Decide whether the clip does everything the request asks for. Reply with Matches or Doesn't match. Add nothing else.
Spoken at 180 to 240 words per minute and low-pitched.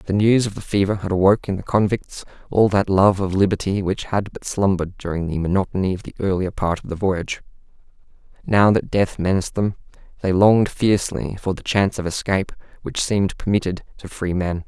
Matches